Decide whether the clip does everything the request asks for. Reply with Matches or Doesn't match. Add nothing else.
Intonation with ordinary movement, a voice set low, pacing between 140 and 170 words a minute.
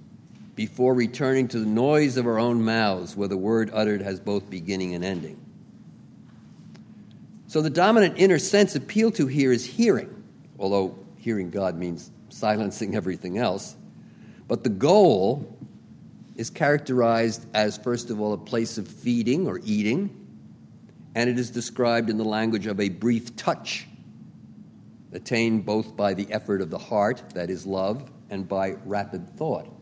Matches